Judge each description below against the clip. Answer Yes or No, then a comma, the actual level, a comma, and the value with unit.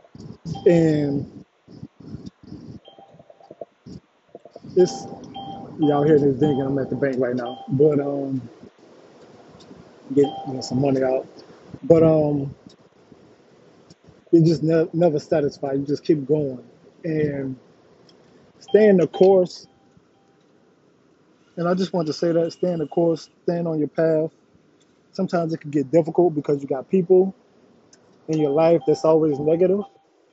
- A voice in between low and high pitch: Yes, medium, 155 Hz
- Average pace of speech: No, slow, 130 wpm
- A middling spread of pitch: Yes, average, 3.2 semitones